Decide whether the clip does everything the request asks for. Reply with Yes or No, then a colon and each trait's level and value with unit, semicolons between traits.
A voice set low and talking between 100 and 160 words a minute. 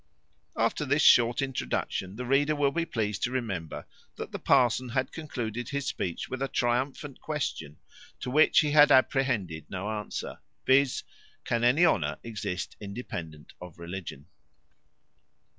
Yes: low, 120 Hz; average, 140 wpm